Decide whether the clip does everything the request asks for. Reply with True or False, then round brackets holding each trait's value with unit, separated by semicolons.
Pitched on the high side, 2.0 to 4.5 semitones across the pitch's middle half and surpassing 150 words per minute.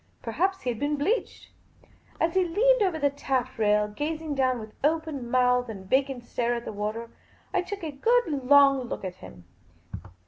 False (275 Hz; 5.5 semitones; 180 wpm)